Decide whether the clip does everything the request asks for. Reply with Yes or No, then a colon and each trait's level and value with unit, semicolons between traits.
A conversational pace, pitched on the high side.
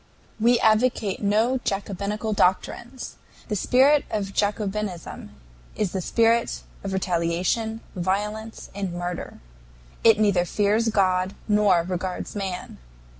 No: slow, 110 wpm; high, 205 Hz